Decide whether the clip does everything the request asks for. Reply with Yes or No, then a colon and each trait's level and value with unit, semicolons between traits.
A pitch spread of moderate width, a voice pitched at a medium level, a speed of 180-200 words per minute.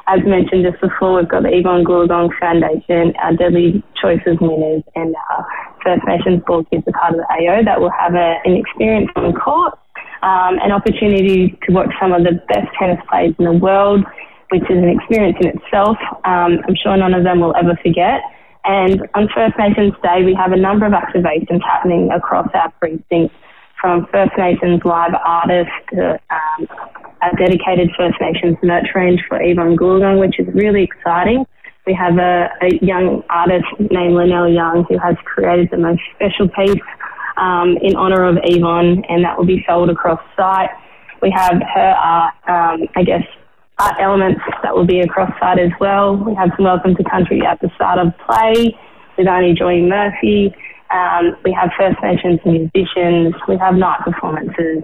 No: narrow, 1.7 semitones; medium, 180 Hz; average, 185 wpm